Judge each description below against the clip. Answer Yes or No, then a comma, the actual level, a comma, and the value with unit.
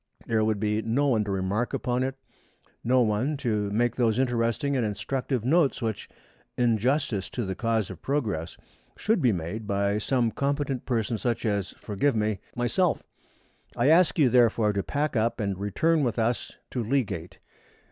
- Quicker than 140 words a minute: Yes, average, 170 wpm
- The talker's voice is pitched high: No, low, 115 Hz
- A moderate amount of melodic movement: Yes, average, 3.9 semitones